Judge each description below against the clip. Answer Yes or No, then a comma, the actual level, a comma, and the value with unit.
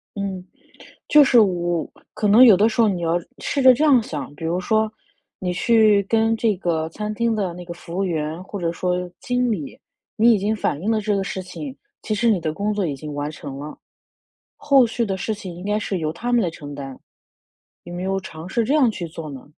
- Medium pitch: No, high, 195 Hz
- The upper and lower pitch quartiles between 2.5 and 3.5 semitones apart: No, average, 4.7 semitones